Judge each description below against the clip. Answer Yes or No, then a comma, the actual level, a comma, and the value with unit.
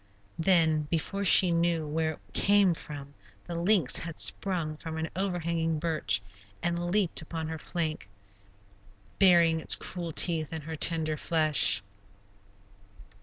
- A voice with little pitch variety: Yes, narrow, 1.8 semitones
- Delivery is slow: Yes, slow, 130 wpm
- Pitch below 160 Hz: No, medium, 165 Hz